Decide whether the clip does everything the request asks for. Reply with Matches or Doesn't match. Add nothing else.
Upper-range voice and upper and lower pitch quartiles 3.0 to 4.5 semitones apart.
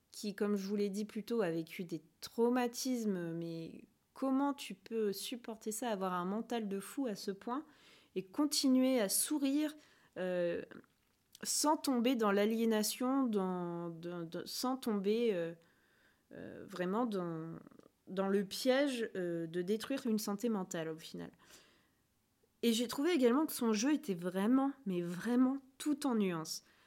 Doesn't match